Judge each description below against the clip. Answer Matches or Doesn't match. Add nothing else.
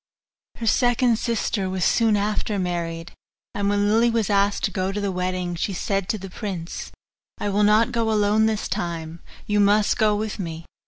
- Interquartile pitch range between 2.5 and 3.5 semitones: Matches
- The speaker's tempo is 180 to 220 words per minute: Matches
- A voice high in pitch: Matches